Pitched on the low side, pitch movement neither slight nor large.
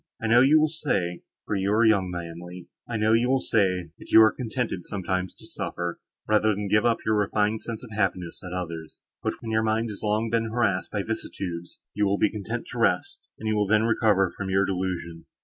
Yes: low, 105 Hz; average, 3.3 semitones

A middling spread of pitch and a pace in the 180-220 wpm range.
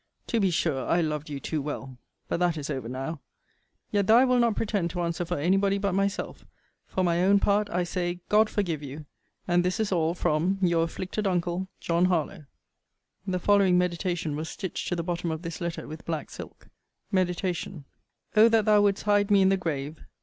Yes: average, 3.4 semitones; fast, 205 wpm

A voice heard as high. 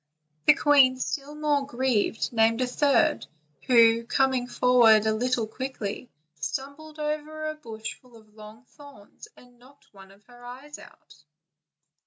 Yes: very high, 250 Hz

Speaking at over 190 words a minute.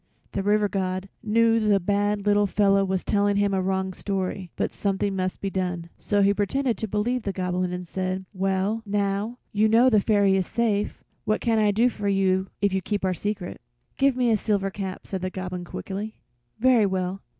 Yes: average, 200 wpm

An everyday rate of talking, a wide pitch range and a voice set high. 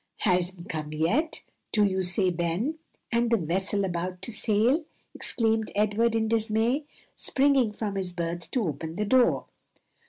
No: average, 150 wpm; average, 4.5 semitones; high, 205 Hz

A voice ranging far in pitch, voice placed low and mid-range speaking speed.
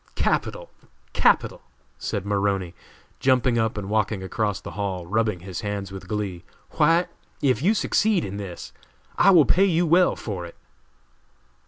Yes: wide, 6.2 semitones; low, 105 Hz; average, 150 wpm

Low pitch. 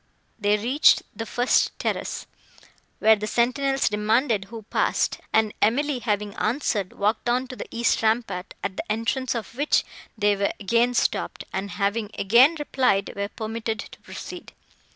No: high, 220 Hz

